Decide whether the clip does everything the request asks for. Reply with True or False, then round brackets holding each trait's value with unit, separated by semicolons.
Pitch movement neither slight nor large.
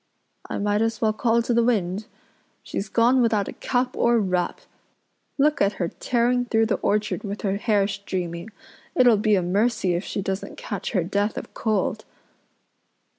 True (3.1 semitones)